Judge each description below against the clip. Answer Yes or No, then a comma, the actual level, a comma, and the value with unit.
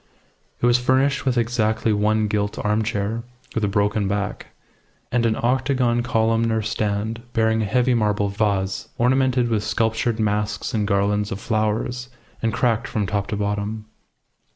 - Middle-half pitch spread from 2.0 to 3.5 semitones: Yes, narrow, 2.4 semitones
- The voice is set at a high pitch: No, low, 110 Hz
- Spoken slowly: No, average, 150 wpm